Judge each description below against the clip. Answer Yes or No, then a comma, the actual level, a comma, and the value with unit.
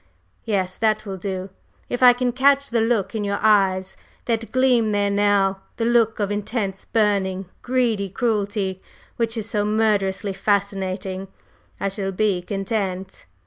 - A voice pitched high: Yes, high, 205 Hz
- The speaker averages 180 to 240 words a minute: No, average, 145 wpm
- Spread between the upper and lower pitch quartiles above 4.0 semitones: No, average, 2.7 semitones